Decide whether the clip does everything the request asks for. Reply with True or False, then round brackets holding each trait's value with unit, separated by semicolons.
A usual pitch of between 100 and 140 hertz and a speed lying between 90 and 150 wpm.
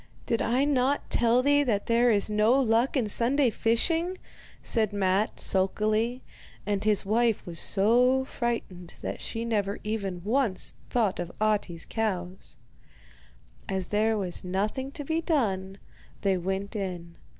False (215 Hz; 140 wpm)